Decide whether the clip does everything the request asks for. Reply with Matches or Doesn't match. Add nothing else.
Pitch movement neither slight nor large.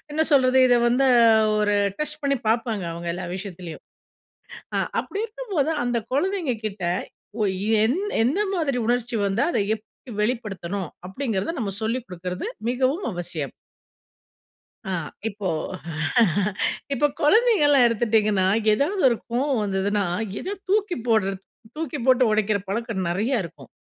Doesn't match